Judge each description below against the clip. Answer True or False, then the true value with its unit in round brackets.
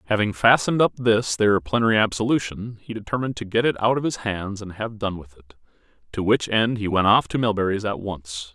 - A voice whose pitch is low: True (110 Hz)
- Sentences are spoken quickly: True (220 wpm)